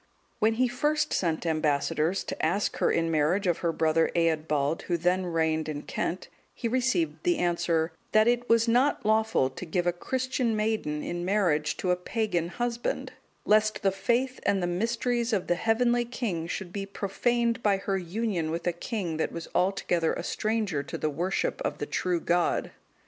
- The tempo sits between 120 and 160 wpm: No, average, 180 wpm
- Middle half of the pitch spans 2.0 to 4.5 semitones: No, wide, 5.4 semitones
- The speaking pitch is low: No, medium, 185 Hz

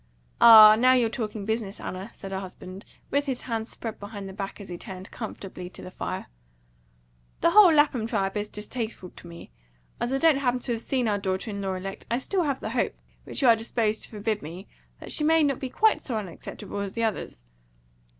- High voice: Yes, high, 220 Hz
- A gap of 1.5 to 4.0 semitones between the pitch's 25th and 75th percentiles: No, average, 4.4 semitones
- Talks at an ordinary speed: No, fast, 210 wpm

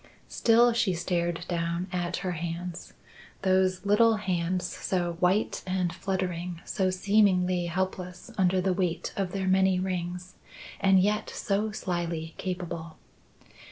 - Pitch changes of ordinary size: No, narrow, 1.5 semitones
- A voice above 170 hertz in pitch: Yes, medium, 185 Hz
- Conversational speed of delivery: No, slow, 125 wpm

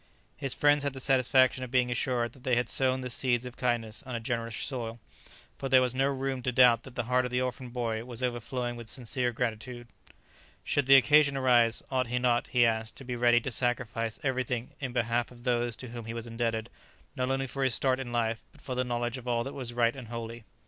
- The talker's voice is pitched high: No, low, 125 Hz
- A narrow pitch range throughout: Yes, narrow, 1.6 semitones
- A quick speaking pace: Yes, fast, 235 wpm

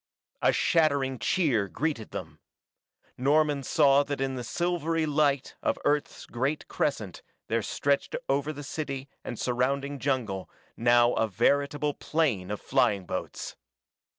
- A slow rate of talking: Yes, slow, 130 wpm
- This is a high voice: No, medium, 140 Hz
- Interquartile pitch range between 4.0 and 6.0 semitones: No, average, 3.5 semitones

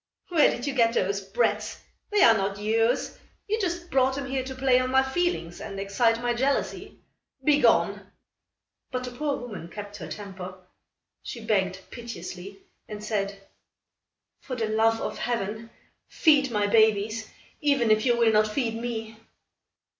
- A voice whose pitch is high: Yes, high, 225 Hz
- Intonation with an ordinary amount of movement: Yes, average, 4.0 semitones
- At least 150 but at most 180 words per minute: Yes, average, 155 wpm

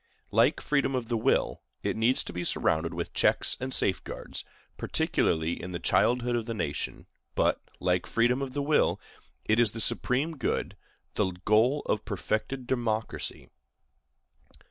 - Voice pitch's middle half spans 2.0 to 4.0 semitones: No, wide, 5.4 semitones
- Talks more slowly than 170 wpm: Yes, average, 150 wpm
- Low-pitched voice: Yes, low, 115 Hz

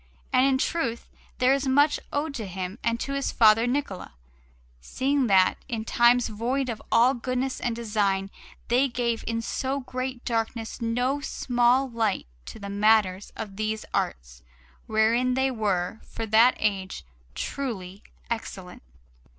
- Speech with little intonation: No, average, 3.3 semitones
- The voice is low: No, high, 230 Hz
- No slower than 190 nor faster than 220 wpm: No, average, 145 wpm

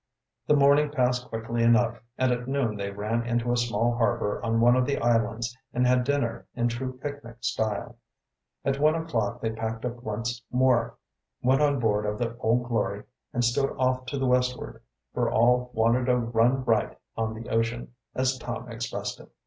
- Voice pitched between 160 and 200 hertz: No, low, 120 Hz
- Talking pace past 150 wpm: Yes, average, 185 wpm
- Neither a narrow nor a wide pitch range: No, narrow, 1.9 semitones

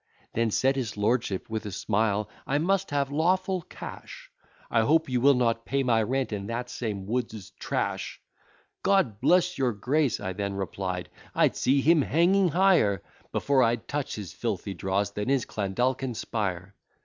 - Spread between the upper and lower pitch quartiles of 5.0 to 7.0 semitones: Yes, wide, 5.4 semitones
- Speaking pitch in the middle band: No, low, 120 Hz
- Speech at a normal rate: Yes, average, 165 wpm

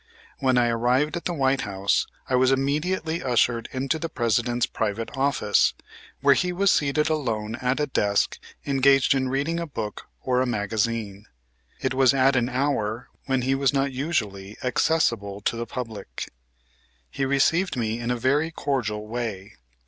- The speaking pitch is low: Yes, low, 130 Hz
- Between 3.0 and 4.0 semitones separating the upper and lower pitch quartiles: Yes, average, 3.5 semitones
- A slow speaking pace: No, average, 165 wpm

